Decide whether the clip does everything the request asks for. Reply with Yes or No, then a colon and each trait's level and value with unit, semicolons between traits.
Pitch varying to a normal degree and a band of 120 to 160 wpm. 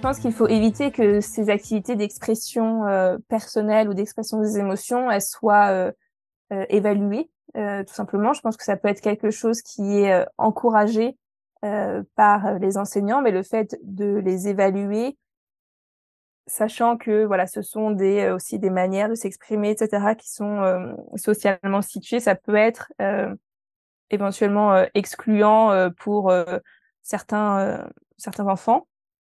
No: narrow, 1.8 semitones; average, 155 wpm